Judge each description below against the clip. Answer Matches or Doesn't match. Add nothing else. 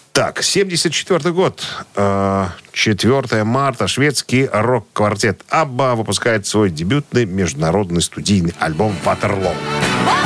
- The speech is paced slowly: Matches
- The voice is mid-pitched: Doesn't match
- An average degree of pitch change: Doesn't match